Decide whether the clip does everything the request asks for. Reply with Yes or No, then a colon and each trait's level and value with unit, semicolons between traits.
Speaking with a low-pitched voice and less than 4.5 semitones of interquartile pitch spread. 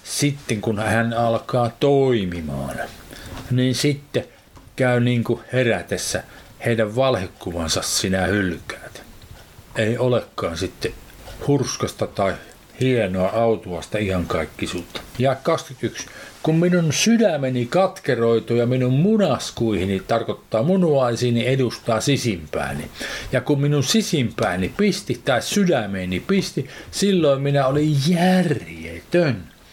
No: low, 125 Hz; average, 4.8 semitones